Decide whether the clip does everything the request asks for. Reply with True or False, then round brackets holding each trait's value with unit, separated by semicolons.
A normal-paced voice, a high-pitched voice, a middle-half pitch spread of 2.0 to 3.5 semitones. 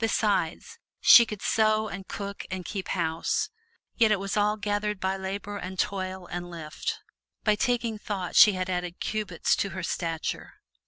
True (165 wpm; 195 Hz; 2.6 semitones)